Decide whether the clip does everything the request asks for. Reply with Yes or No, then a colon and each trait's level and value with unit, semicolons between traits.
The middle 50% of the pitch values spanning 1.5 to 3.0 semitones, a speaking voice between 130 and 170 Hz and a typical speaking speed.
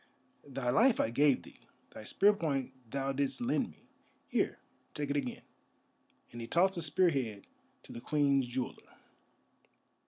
No: average, 4.8 semitones; medium, 140 Hz; average, 155 wpm